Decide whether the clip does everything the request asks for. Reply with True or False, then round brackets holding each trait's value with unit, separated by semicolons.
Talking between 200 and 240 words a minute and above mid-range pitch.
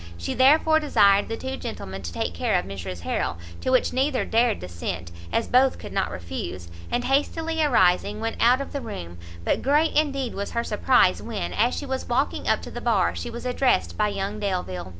True (205 wpm; 225 Hz)